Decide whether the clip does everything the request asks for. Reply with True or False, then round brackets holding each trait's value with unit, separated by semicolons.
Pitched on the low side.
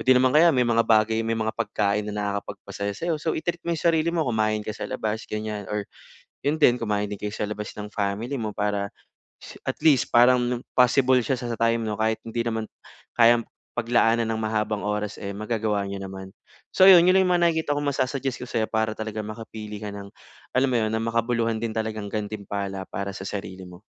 True (110 Hz)